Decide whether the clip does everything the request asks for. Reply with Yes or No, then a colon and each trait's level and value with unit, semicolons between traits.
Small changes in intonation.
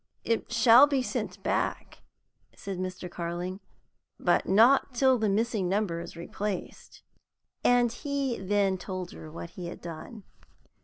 No: average, 4.7 semitones